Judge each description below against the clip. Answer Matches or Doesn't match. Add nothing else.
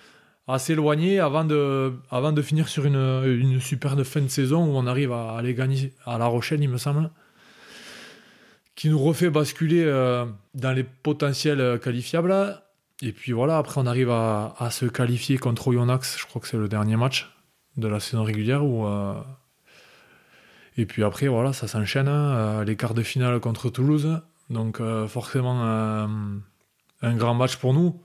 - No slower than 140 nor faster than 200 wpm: Matches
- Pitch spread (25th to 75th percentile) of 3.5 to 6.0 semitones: Matches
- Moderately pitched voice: Doesn't match